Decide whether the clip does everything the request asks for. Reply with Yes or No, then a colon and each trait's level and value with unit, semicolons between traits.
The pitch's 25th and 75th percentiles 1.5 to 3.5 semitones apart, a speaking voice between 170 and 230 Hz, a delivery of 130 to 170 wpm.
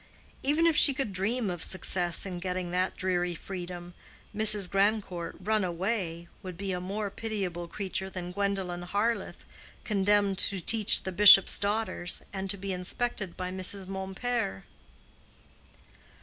Yes: narrow, 2.4 semitones; high, 190 Hz; average, 140 wpm